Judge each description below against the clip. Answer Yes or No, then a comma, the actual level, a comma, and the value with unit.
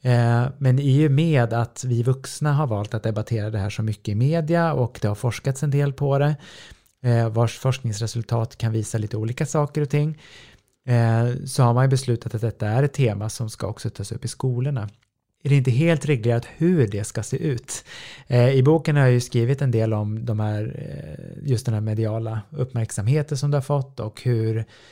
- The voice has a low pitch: Yes, low, 120 Hz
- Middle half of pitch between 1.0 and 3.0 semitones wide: No, average, 3.8 semitones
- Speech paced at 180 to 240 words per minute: Yes, average, 200 wpm